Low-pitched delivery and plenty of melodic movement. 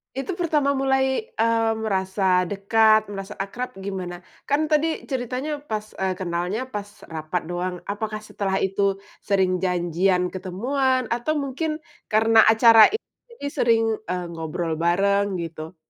No: high, 205 Hz; wide, 5.7 semitones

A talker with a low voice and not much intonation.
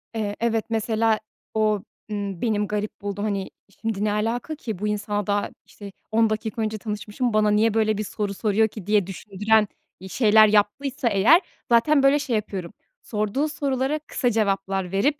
No: high, 215 Hz; narrow, 1.9 semitones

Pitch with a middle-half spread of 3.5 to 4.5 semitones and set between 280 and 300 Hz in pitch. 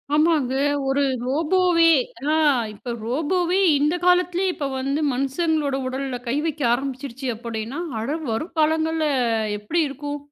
Yes: average, 3.8 semitones; very high, 290 Hz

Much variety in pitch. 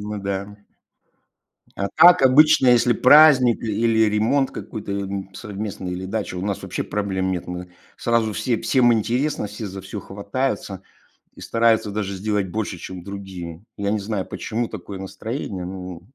No: average, 3.2 semitones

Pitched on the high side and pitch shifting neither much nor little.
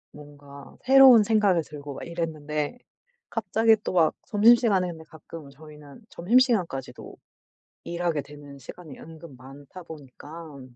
No: medium, 160 Hz; average, 4.3 semitones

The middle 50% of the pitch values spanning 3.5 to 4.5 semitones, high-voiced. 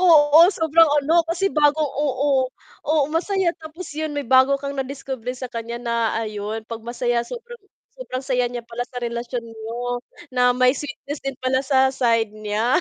Yes: average, 3.8 semitones; very high, 260 Hz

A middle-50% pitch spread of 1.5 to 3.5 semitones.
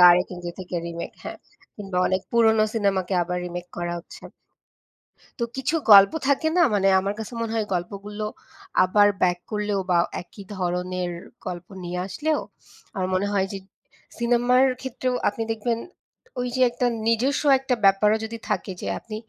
No: average, 4.1 semitones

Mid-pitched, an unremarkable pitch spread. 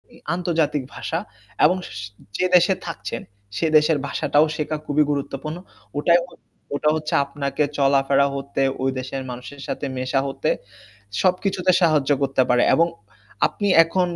Yes: medium, 145 Hz; average, 3.3 semitones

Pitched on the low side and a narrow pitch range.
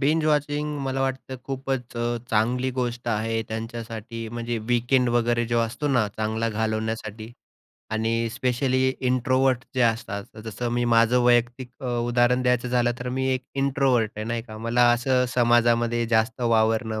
Yes: low, 120 Hz; narrow, 2.0 semitones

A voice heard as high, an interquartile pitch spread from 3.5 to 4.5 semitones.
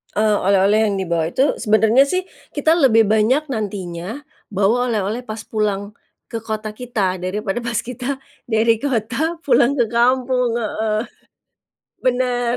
No: high, 225 Hz; average, 2.9 semitones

